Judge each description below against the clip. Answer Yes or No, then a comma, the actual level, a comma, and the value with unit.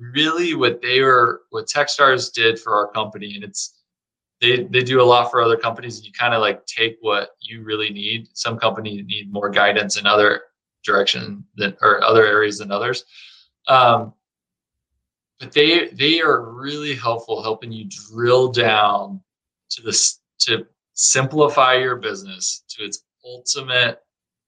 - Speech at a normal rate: Yes, average, 155 wpm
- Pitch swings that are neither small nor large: Yes, average, 3.9 semitones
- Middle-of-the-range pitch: No, low, 115 Hz